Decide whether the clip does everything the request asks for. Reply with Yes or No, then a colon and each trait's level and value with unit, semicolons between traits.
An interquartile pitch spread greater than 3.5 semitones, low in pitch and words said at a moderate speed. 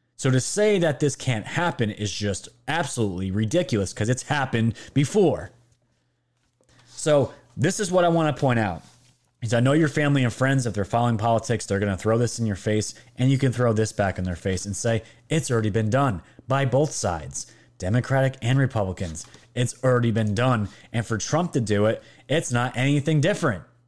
Yes: average, 4.2 semitones; low, 120 Hz; average, 195 wpm